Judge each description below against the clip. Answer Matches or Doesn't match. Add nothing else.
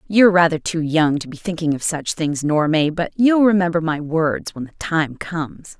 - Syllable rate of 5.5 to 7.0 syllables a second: Doesn't match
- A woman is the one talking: Matches